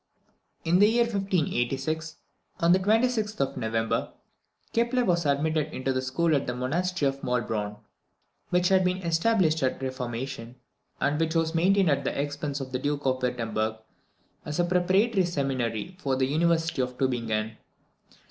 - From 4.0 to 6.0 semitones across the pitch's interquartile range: Yes, wide, 5.6 semitones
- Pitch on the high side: No, medium, 150 Hz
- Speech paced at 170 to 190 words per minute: No, average, 155 wpm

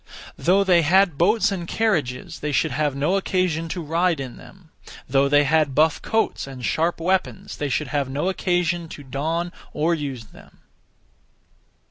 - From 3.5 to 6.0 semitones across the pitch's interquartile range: Yes, average, 4.0 semitones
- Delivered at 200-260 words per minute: No, average, 165 wpm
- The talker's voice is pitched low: No, medium, 160 Hz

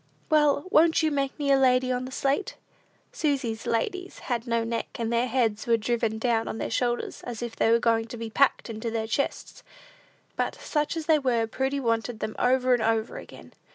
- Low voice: No, high, 240 Hz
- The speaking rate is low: No, fast, 205 wpm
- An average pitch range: Yes, average, 3.3 semitones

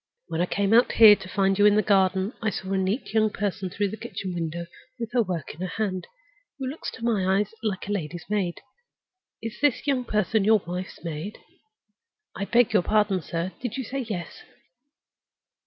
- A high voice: Yes, high, 200 Hz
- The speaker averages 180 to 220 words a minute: Yes, average, 200 wpm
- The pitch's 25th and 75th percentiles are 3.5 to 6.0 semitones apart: No, average, 3.0 semitones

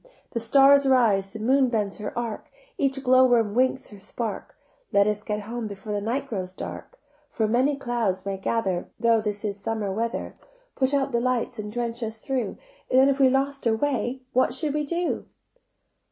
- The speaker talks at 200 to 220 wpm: No, average, 180 wpm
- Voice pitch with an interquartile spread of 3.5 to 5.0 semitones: Yes, average, 3.9 semitones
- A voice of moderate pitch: No, high, 235 Hz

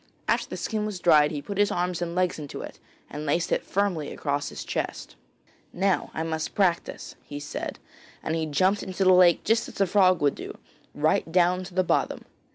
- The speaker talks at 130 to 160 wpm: No, fast, 205 wpm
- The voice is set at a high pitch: No, medium, 175 Hz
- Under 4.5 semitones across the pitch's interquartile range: Yes, average, 3.2 semitones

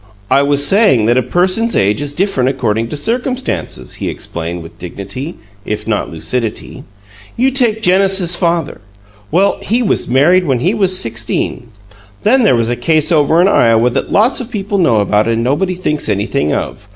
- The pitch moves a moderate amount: No, wide, 9.0 semitones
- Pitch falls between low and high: Yes, medium, 145 Hz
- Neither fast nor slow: Yes, average, 175 wpm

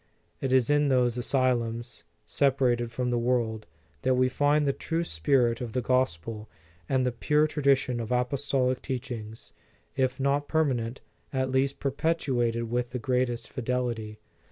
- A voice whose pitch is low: Yes, low, 125 Hz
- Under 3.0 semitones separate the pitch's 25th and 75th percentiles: Yes, narrow, 2.4 semitones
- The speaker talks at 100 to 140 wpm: No, average, 155 wpm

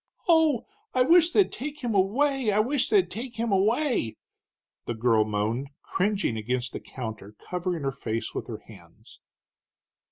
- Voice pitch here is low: No, high, 200 Hz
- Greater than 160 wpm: No, average, 155 wpm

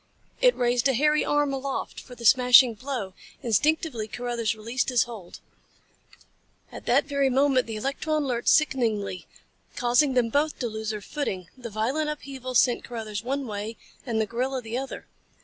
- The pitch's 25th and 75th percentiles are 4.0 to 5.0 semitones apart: No, average, 3.5 semitones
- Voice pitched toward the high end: Yes, high, 245 Hz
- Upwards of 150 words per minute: Yes, average, 165 wpm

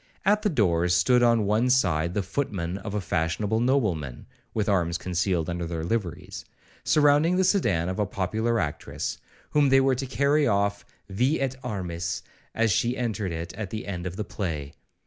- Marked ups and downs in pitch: Yes, wide, 6.1 semitones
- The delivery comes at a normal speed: Yes, average, 180 wpm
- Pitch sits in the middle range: No, low, 100 Hz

